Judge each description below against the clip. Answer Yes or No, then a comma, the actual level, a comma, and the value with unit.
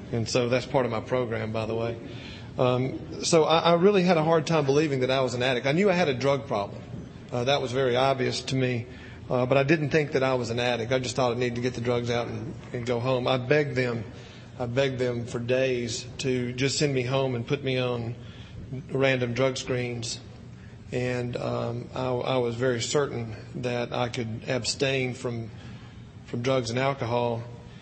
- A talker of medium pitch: No, low, 125 Hz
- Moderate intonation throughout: No, narrow, 1.9 semitones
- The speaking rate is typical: No, fast, 215 wpm